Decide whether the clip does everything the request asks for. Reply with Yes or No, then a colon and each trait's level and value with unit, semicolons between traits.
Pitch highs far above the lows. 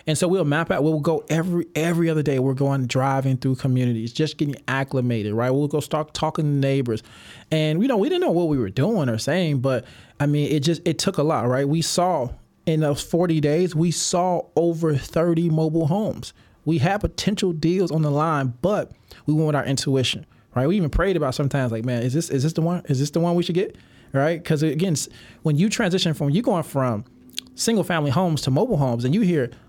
No: average, 4.0 semitones